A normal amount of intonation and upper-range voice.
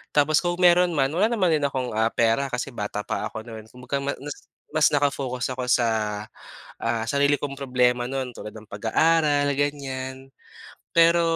No: average, 3.1 semitones; low, 135 Hz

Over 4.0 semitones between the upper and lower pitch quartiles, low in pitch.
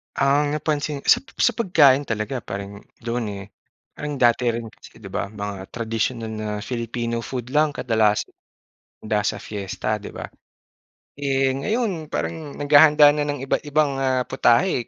Yes: average, 4.7 semitones; low, 130 Hz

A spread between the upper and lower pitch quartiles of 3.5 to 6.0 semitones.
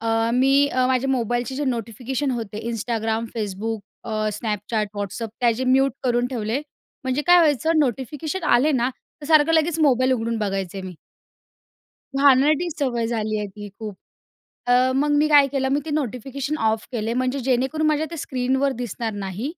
Yes: average, 3.8 semitones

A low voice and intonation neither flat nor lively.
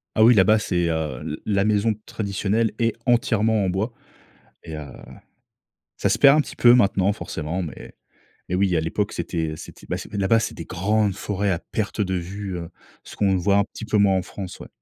Yes: low, 100 Hz; average, 3.1 semitones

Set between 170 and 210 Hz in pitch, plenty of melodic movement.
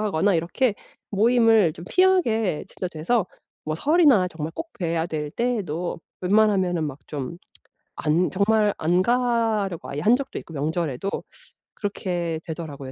Yes: medium, 185 Hz; wide, 5.7 semitones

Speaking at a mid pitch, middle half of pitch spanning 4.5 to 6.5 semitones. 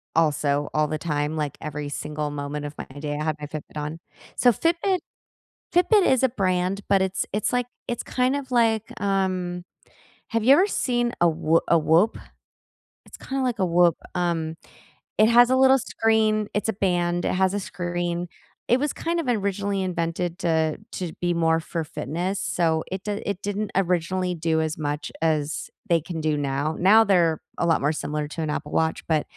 Yes: medium, 175 Hz; average, 5.1 semitones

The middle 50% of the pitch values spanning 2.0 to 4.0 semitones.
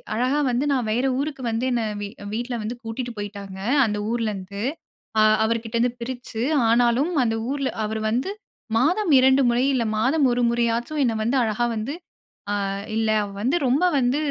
Yes: average, 2.8 semitones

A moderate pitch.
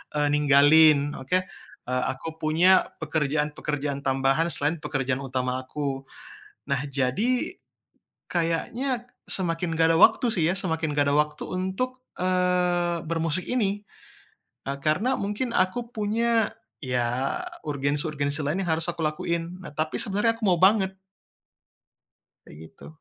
Yes: medium, 160 Hz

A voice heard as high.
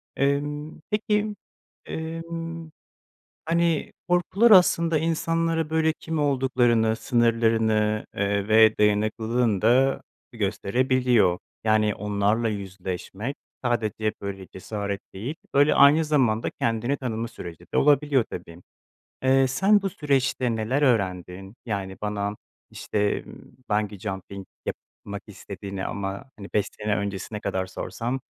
No: low, 115 Hz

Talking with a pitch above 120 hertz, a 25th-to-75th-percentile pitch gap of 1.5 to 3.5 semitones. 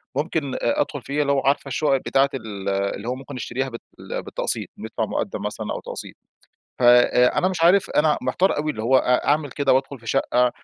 Yes: low, 135 Hz; average, 3.0 semitones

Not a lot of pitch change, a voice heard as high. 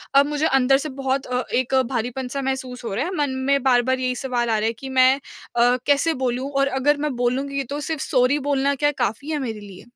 Yes: narrow, 2.1 semitones; very high, 265 Hz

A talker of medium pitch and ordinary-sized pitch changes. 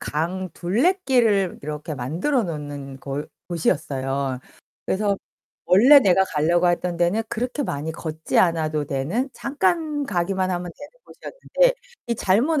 No: medium, 180 Hz; wide, 7.9 semitones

